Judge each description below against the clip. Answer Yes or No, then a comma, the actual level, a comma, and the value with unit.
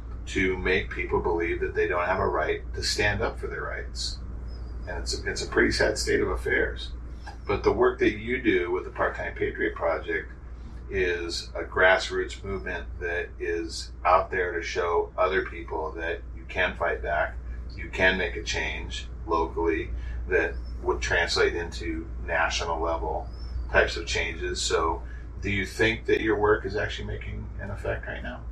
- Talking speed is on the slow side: No, average, 175 wpm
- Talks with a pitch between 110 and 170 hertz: No, very low, 85 Hz